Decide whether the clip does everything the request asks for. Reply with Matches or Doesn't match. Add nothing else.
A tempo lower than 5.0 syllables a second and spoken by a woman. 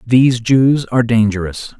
Doesn't match